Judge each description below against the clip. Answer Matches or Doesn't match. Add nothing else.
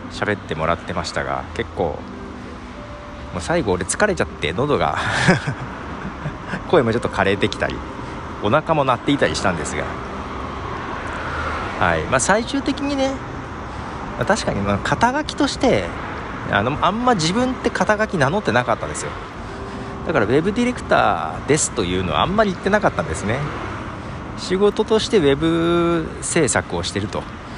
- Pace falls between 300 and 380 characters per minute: Matches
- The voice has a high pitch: Doesn't match